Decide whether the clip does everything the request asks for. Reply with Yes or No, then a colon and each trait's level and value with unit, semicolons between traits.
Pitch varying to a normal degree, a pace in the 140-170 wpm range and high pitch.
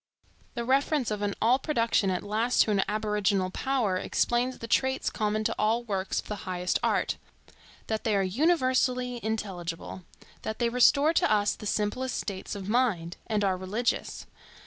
Yes: average, 3.9 semitones; average, 160 wpm; high, 215 Hz